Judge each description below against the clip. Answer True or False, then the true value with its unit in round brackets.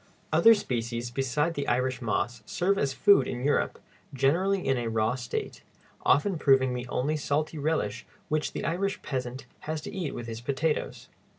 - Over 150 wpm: True (170 wpm)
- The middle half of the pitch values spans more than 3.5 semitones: True (4.5 semitones)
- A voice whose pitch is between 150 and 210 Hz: False (135 Hz)